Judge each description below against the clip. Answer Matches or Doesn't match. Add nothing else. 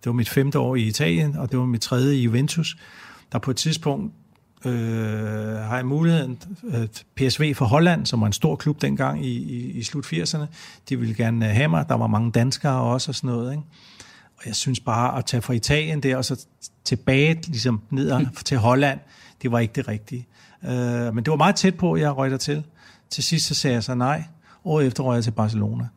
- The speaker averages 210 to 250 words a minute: Matches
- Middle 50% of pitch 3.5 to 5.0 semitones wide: Matches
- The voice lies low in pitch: Matches